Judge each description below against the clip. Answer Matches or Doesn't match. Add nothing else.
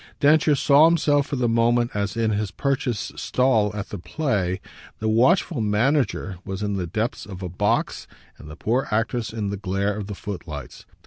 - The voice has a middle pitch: Doesn't match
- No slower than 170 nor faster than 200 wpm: Matches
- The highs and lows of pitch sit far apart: Doesn't match